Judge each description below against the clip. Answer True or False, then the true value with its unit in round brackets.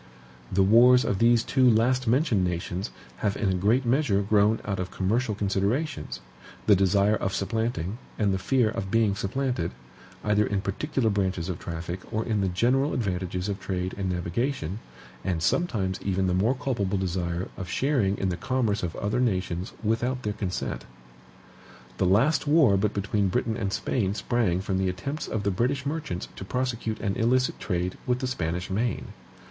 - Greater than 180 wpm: False (175 wpm)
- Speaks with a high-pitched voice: False (100 Hz)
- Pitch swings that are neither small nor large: True (4.3 semitones)